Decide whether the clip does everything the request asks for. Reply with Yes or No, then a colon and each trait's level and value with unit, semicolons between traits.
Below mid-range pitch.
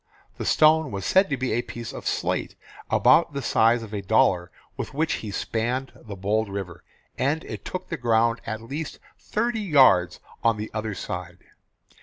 Yes: low, 115 Hz